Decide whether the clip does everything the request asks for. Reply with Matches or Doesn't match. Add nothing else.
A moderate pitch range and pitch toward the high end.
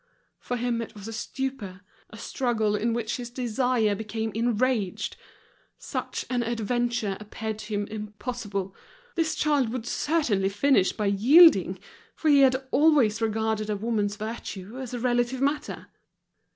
Matches